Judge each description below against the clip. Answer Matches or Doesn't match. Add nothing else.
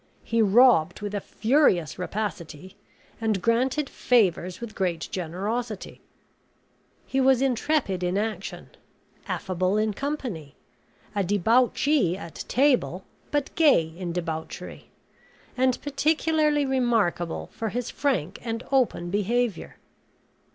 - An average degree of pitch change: Doesn't match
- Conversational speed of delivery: Doesn't match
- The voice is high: Matches